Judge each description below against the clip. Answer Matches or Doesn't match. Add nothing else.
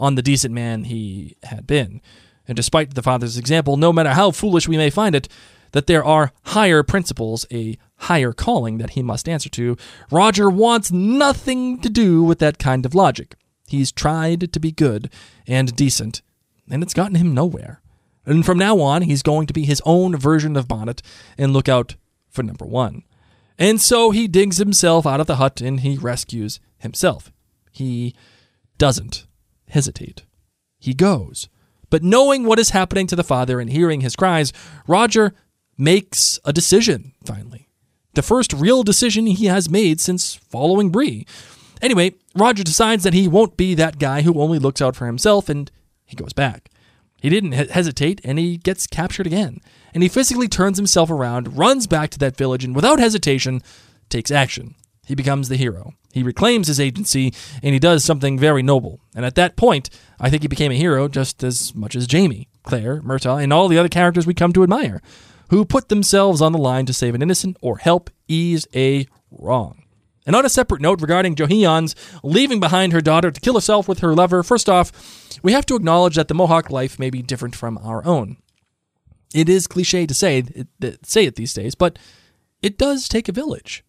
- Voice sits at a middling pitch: Matches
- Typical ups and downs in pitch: Doesn't match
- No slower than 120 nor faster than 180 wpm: Doesn't match